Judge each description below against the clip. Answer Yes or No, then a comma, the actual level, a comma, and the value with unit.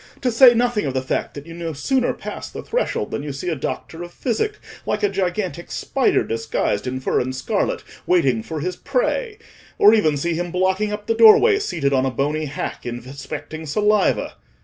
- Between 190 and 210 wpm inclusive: Yes, average, 195 wpm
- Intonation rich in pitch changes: Yes, wide, 7.3 semitones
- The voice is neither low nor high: Yes, medium, 175 Hz